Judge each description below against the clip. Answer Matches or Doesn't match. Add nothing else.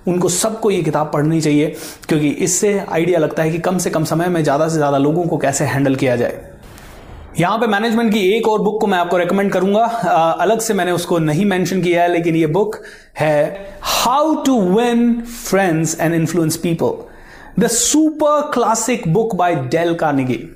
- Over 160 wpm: Matches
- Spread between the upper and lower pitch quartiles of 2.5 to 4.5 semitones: Doesn't match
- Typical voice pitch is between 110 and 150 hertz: Doesn't match